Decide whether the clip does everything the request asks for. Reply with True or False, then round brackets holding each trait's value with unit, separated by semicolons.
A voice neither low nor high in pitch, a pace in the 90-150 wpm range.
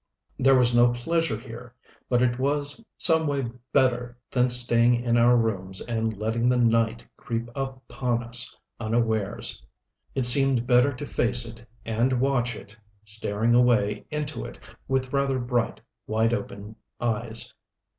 False (120 Hz; 145 wpm)